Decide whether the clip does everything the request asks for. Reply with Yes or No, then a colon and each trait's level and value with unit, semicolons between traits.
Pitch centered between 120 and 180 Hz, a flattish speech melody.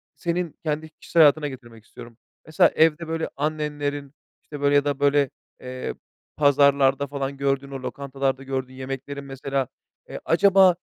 Yes: medium, 140 Hz; narrow, 2.0 semitones